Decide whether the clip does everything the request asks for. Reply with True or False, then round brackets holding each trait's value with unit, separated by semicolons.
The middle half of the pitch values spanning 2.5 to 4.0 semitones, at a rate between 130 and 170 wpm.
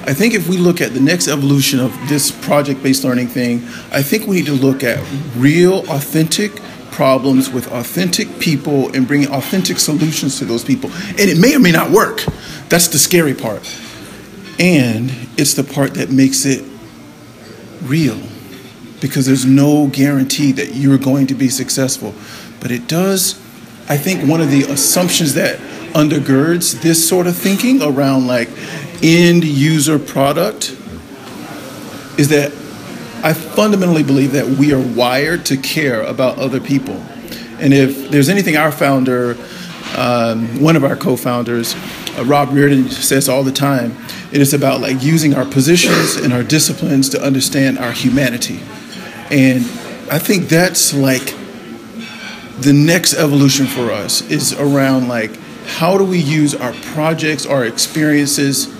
True (3.3 semitones; 155 wpm)